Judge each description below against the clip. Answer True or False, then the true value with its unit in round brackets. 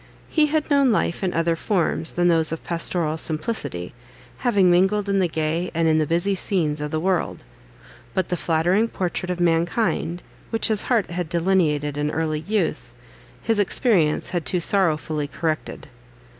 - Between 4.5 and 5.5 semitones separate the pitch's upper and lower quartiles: False (3.6 semitones)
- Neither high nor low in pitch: True (175 Hz)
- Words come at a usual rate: True (165 wpm)